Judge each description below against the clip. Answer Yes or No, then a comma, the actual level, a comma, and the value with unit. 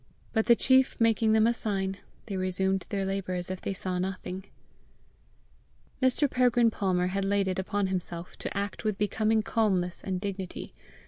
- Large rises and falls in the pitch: No, average, 2.9 semitones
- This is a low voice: No, high, 195 Hz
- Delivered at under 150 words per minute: No, average, 170 wpm